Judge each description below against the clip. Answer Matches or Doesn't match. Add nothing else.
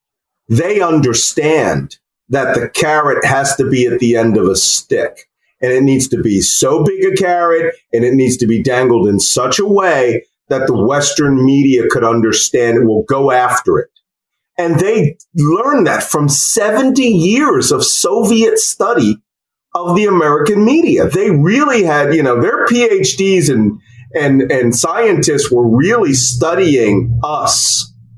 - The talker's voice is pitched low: Doesn't match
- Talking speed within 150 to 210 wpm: Matches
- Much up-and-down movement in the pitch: Matches